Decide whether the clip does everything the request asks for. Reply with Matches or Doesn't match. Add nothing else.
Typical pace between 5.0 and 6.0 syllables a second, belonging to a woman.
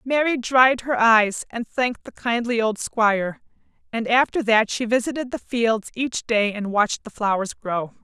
Doesn't match